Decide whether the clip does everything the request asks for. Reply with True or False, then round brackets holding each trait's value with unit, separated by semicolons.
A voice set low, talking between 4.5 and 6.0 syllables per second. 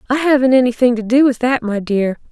False (245 Hz; 5.9 syllables/s)